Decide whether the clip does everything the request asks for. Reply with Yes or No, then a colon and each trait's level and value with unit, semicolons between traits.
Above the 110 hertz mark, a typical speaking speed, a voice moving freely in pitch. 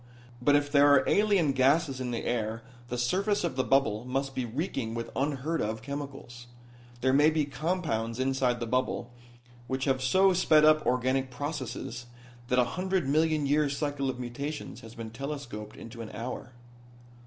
No: low, 135 Hz; average, 170 wpm; average, 3.5 semitones